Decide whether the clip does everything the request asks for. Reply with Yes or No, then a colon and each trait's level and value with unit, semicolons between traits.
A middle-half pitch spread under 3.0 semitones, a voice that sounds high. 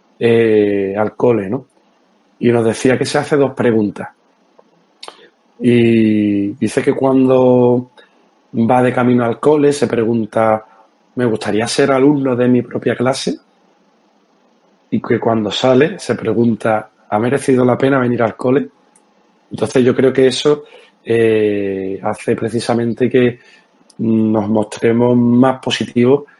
No: narrow, 2.6 semitones; low, 120 Hz